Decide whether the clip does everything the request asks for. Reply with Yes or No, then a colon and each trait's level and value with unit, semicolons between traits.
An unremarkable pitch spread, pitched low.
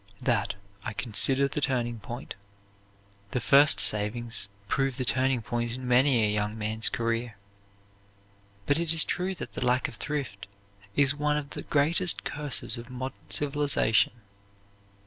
Yes: average, 3.7 semitones; low, 125 Hz